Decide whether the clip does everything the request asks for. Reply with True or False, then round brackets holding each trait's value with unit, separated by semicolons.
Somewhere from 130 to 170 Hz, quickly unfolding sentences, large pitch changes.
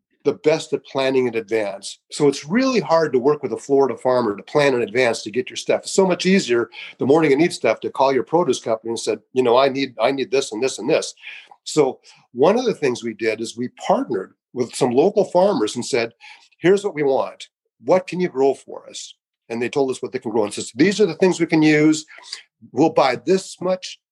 True (140 Hz; 245 wpm; 7.3 semitones)